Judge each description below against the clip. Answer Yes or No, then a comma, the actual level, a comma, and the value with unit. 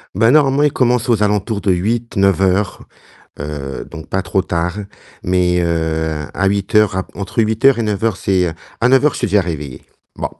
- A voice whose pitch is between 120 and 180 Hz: No, low, 100 Hz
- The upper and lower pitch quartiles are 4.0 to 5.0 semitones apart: Yes, average, 4.5 semitones